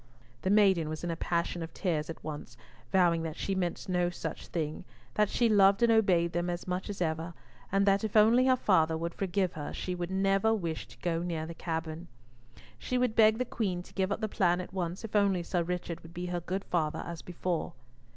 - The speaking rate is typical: No, fast, 225 wpm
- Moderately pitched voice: Yes, medium, 180 Hz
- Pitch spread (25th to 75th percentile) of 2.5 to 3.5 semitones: Yes, average, 2.8 semitones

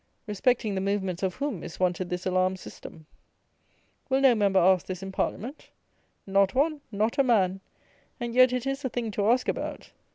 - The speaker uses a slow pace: No, average, 185 wpm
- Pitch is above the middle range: Yes, high, 205 Hz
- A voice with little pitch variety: No, average, 5.1 semitones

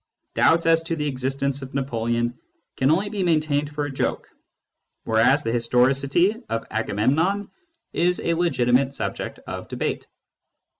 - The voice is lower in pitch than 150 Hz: Yes, medium, 140 Hz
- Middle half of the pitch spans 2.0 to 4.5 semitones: No, average, 4.9 semitones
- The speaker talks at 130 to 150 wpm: Yes, average, 140 wpm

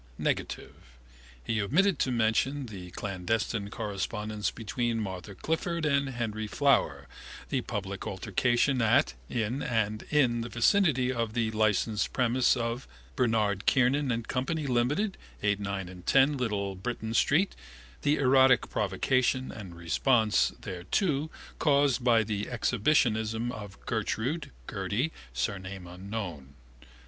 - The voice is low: Yes, low, 115 Hz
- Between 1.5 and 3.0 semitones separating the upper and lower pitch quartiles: No, average, 4.4 semitones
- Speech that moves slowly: Yes, slow, 120 wpm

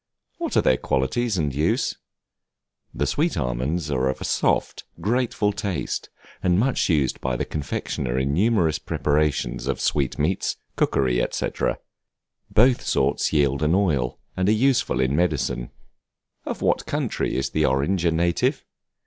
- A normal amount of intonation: No, wide, 6.2 semitones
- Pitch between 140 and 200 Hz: No, very low, 75 Hz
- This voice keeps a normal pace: Yes, average, 150 wpm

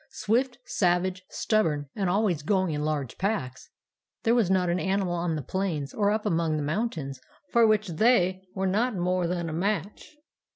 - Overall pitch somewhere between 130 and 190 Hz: Yes, medium, 185 Hz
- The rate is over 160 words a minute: Yes, average, 175 wpm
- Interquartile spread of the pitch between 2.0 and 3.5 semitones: No, average, 4.5 semitones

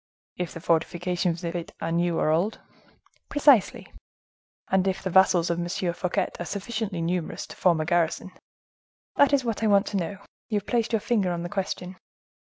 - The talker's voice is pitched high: No, medium, 180 Hz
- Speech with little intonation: No, average, 3.0 semitones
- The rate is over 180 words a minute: Yes, average, 190 wpm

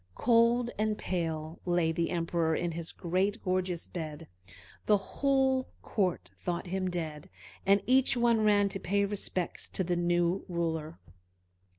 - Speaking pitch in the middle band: Yes, medium, 180 Hz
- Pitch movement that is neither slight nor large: Yes, average, 3.7 semitones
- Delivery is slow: No, average, 145 wpm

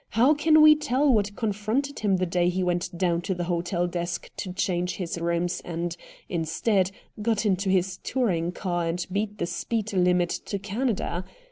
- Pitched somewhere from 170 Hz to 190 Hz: Yes, medium, 185 Hz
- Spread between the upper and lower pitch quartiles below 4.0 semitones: Yes, average, 3.6 semitones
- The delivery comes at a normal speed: Yes, average, 175 wpm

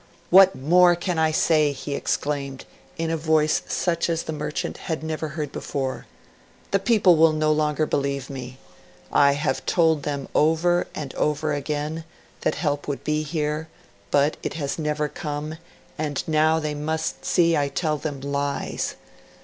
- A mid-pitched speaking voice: Yes, medium, 155 Hz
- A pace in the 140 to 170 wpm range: Yes, average, 160 wpm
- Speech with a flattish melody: Yes, narrow, 1.8 semitones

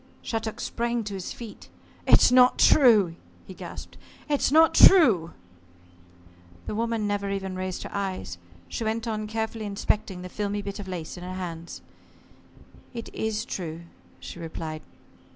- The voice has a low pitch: No, high, 205 Hz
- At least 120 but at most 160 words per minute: Yes, average, 150 wpm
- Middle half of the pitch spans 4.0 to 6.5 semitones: No, average, 3.6 semitones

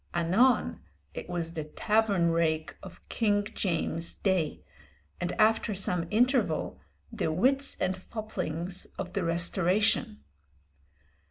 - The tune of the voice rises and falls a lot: No, average, 4.3 semitones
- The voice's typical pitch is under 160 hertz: No, medium, 185 Hz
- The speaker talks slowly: Yes, slow, 110 wpm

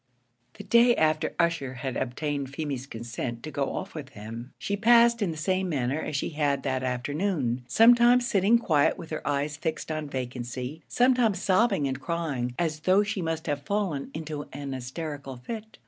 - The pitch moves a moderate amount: No, wide, 6.0 semitones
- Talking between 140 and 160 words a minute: No, average, 180 wpm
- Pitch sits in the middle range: Yes, medium, 155 Hz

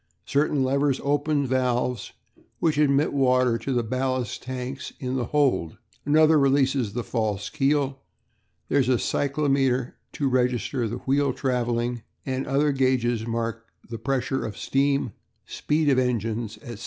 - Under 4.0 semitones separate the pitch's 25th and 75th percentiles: Yes, narrow, 2.6 semitones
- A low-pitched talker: Yes, low, 130 Hz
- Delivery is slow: No, average, 145 wpm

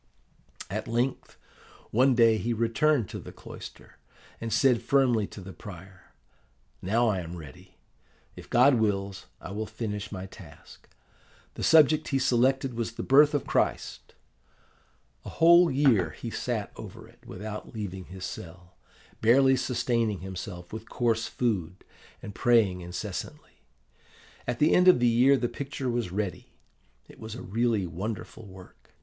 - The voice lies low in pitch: Yes, low, 115 Hz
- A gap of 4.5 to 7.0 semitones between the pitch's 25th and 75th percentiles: Yes, average, 4.8 semitones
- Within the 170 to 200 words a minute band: No, average, 150 wpm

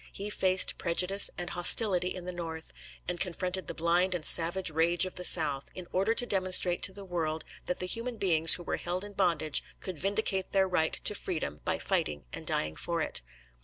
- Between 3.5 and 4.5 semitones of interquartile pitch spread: No, narrow, 2.4 semitones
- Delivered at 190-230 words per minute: Yes, average, 200 wpm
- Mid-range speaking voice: Yes, medium, 180 Hz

